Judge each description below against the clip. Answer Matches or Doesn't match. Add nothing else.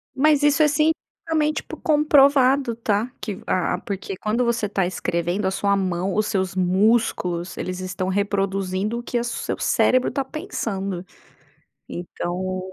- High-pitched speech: Matches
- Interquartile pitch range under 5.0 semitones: Doesn't match